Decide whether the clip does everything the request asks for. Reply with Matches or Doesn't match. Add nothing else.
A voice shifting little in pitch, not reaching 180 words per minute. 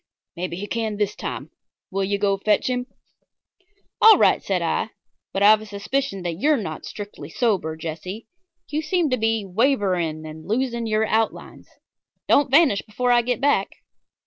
Doesn't match